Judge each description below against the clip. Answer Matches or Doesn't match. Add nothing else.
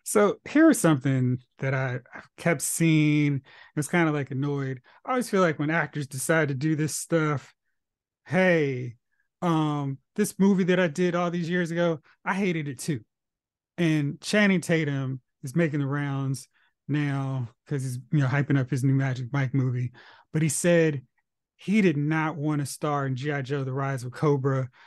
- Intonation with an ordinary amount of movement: Matches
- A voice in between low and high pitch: Matches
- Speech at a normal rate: Matches